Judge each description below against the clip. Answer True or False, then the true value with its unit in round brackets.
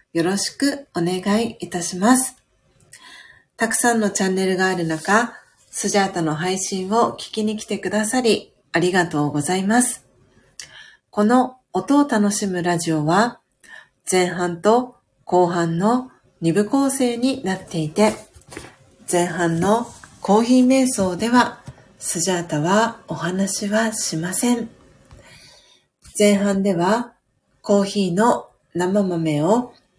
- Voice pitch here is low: False (200 Hz)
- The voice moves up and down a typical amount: True (4.5 semitones)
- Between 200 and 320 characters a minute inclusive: True (235 characters per minute)